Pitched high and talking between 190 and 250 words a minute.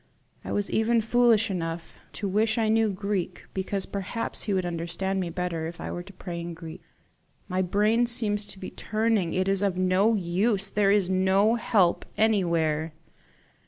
No: high, 195 Hz; average, 165 wpm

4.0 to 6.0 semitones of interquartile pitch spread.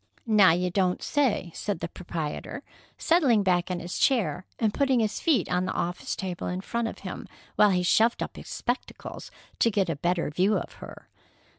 Yes: average, 4.3 semitones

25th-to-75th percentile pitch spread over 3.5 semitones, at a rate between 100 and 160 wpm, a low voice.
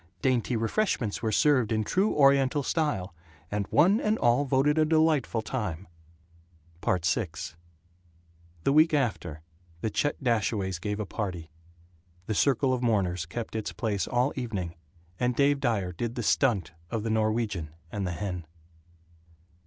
Yes: wide, 5.6 semitones; average, 145 wpm; low, 115 Hz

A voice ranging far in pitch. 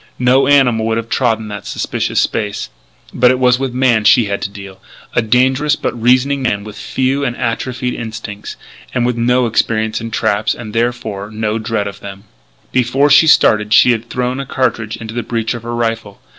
No: narrow, 2.5 semitones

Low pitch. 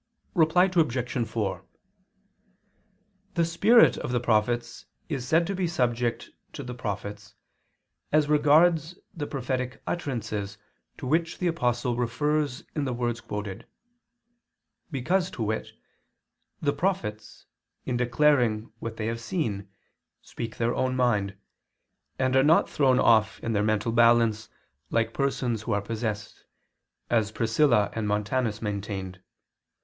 Yes: low, 120 Hz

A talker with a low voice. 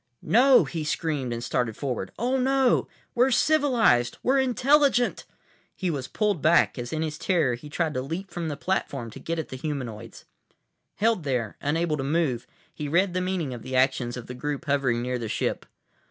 No: medium, 150 Hz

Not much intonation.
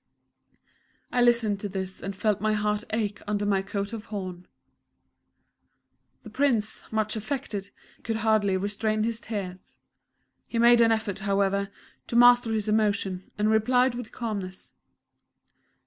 Yes: narrow, 2.2 semitones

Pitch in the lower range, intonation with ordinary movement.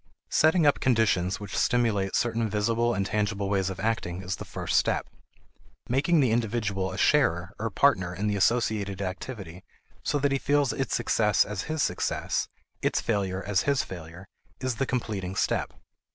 Yes: low, 105 Hz; average, 4.2 semitones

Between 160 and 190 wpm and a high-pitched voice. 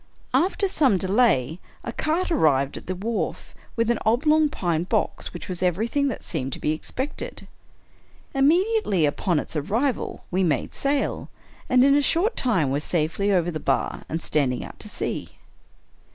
Yes: average, 165 wpm; high, 205 Hz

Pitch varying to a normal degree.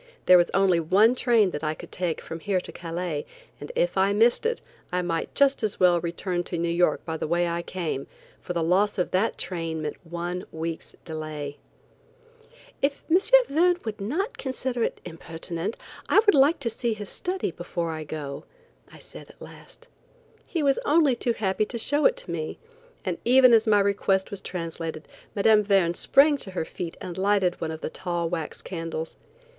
No: wide, 5.8 semitones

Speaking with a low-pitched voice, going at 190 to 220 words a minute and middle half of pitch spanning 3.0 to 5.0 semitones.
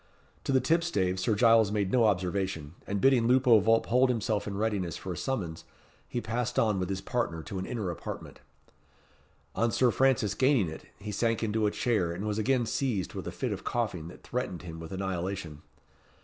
Yes: low, 105 Hz; average, 195 wpm; average, 4.4 semitones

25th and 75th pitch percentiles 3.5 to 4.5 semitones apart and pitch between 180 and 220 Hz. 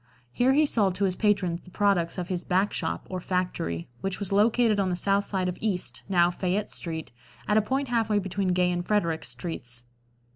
No: average, 2.8 semitones; medium, 185 Hz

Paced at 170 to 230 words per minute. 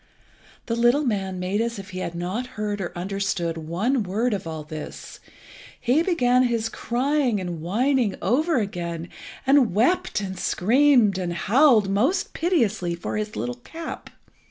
No: average, 155 wpm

